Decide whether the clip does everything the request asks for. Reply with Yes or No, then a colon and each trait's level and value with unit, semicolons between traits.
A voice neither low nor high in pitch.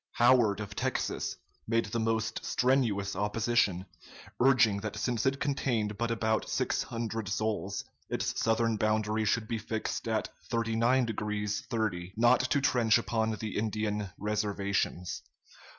No: low, 110 Hz